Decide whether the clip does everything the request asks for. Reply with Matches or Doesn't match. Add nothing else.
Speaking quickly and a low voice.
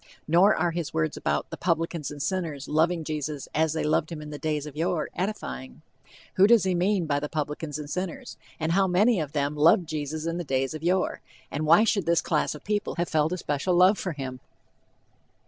Doesn't match